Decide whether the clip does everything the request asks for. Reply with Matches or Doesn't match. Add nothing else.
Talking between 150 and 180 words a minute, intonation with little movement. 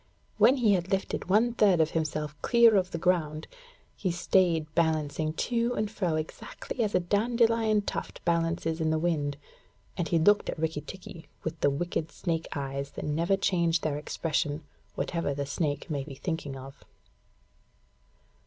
Doesn't match